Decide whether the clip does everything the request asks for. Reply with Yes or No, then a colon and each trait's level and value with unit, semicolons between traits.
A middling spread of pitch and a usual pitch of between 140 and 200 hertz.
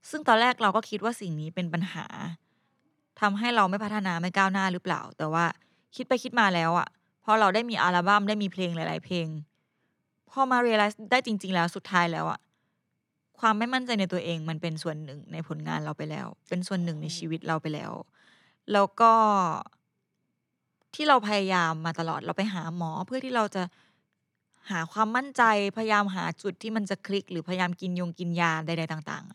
Yes: average, 4.2 semitones; medium, 185 Hz